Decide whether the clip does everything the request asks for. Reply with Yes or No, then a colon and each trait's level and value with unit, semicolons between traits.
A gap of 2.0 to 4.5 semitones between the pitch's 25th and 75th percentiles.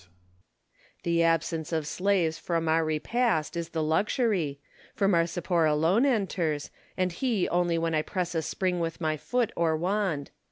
Yes: average, 2.9 semitones